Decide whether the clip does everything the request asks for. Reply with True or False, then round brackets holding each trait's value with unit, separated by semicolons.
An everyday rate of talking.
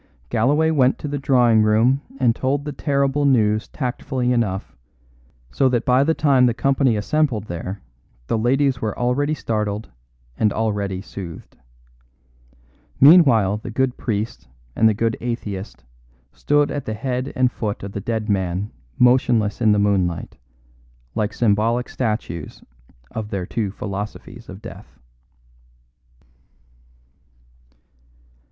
False (130 wpm)